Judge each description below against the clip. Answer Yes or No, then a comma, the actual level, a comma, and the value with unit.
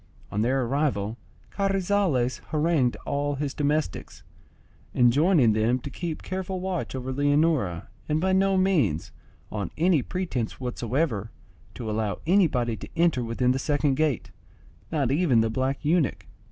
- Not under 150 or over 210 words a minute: No, average, 140 wpm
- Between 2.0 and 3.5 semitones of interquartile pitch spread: No, wide, 5.5 semitones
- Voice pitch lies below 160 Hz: Yes, medium, 140 Hz